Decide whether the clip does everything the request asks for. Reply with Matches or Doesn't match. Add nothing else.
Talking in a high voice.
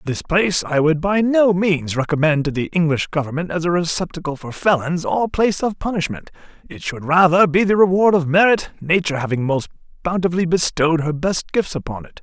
Doesn't match